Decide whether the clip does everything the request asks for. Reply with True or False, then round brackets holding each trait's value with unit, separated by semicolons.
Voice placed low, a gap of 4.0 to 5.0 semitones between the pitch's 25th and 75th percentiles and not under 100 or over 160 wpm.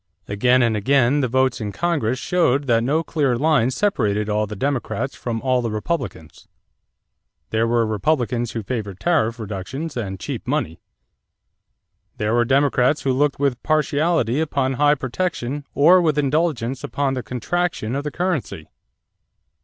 True (130 Hz; 4.4 semitones; 150 wpm)